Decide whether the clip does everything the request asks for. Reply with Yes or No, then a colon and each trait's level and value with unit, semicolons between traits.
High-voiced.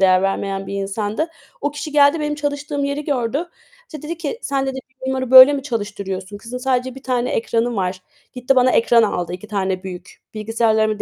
Yes: high, 245 Hz